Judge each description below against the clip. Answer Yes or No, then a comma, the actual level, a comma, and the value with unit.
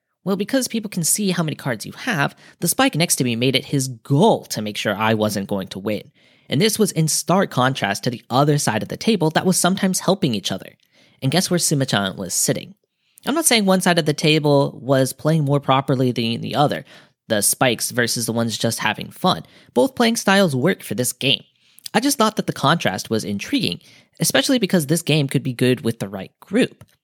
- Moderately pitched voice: Yes, medium, 145 Hz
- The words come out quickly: Yes, fast, 225 wpm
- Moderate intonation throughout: No, wide, 7.0 semitones